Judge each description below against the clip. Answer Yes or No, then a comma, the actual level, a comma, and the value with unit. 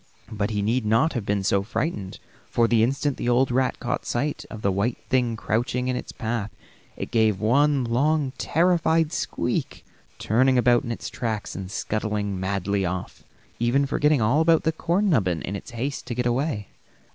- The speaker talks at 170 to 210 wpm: Yes, average, 185 wpm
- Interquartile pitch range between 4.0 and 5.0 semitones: Yes, average, 4.6 semitones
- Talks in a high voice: No, low, 120 Hz